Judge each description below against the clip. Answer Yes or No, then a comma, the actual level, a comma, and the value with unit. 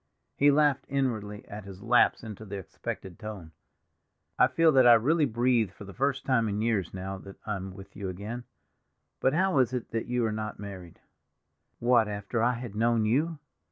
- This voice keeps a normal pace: Yes, average, 190 wpm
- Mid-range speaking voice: No, low, 110 Hz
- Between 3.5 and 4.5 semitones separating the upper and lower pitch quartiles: Yes, average, 3.9 semitones